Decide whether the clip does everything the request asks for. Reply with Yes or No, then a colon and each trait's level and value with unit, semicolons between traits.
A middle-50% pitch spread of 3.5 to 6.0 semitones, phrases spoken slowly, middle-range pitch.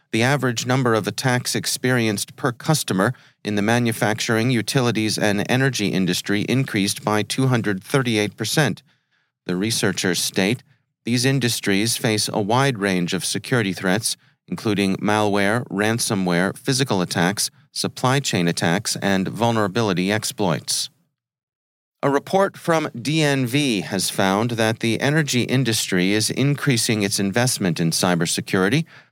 No: average, 4.5 semitones; slow, 115 wpm; low, 115 Hz